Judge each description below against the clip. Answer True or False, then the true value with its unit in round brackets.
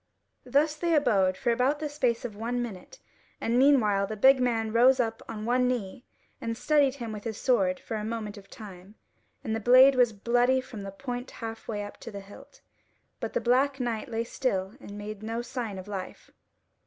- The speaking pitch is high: True (230 Hz)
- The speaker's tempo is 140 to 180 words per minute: False (205 wpm)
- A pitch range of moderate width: True (3.4 semitones)